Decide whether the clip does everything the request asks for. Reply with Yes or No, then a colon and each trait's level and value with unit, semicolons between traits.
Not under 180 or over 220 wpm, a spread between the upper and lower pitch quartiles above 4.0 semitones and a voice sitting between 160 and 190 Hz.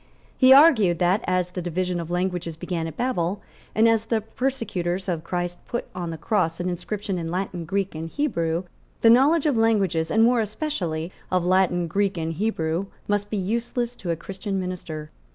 Yes: average, 185 wpm; average, 4.5 semitones; medium, 185 Hz